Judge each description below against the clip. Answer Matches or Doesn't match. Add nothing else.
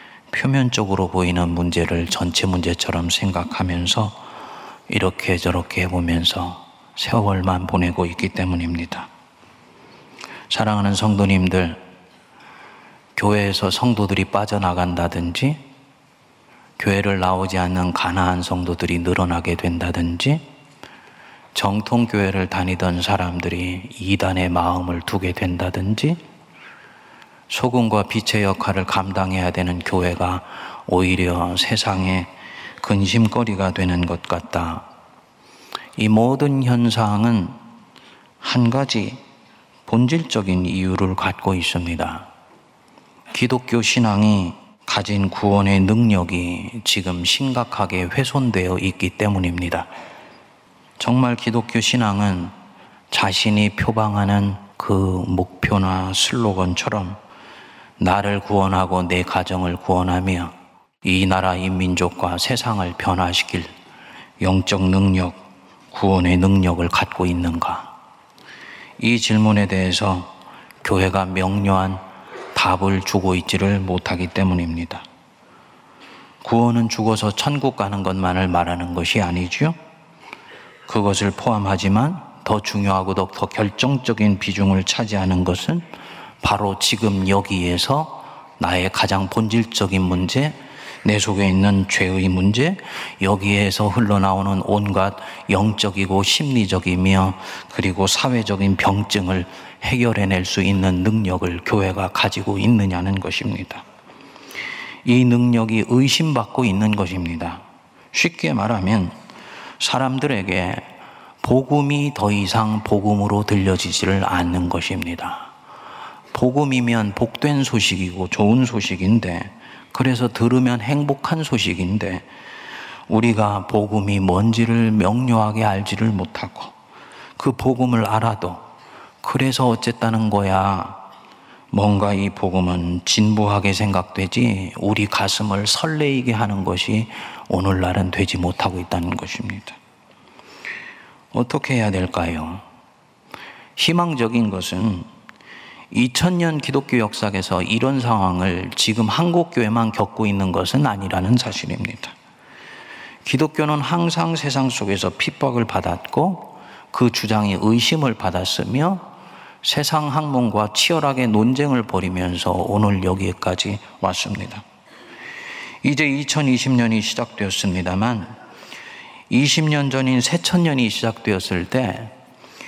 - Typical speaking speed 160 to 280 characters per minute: Matches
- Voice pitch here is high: Doesn't match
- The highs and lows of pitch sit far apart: Doesn't match